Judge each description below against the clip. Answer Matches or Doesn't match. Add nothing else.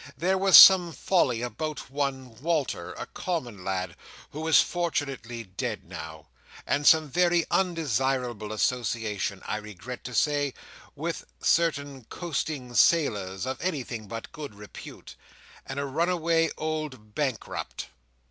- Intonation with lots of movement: Matches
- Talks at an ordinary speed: Doesn't match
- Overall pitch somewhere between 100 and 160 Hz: Matches